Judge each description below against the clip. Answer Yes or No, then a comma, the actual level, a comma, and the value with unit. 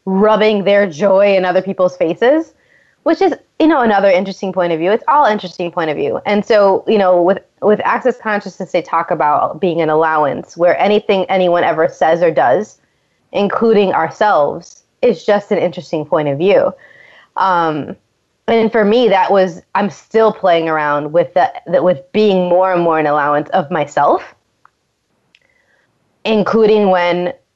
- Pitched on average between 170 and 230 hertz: Yes, high, 190 Hz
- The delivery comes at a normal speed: Yes, average, 165 wpm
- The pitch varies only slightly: No, average, 3.5 semitones